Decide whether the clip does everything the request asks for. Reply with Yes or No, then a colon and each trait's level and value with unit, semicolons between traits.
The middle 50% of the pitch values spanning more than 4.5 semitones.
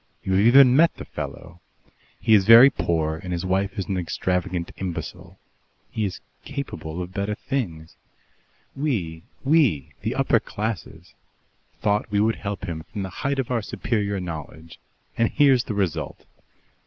Yes: average, 5.1 semitones